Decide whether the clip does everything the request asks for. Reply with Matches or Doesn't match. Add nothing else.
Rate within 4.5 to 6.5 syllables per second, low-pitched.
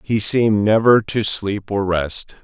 Doesn't match